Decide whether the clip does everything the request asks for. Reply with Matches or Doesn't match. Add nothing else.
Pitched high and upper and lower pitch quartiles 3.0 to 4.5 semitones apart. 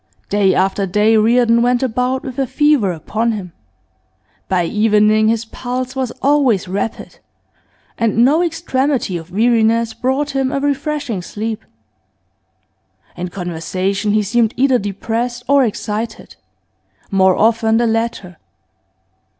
Matches